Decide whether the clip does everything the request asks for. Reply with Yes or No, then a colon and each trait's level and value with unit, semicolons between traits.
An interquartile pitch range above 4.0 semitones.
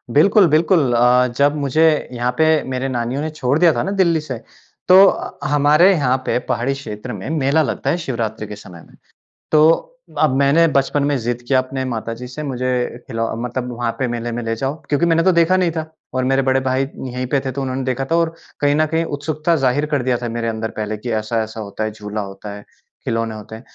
Yes: average, 4.4 semitones